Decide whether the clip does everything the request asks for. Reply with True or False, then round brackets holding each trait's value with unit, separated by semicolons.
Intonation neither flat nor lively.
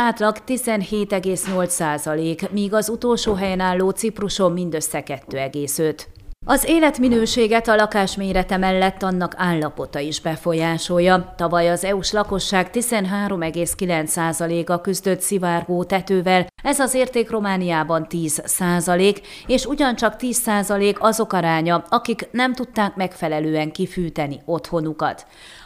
True (4.0 semitones)